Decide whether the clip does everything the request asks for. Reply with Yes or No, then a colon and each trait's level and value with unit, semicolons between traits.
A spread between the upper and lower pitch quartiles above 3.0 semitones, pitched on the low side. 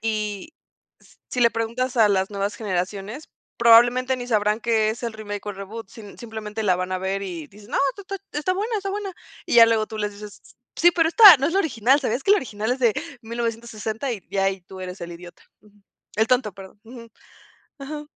No: average, 3.8 semitones; high, 225 Hz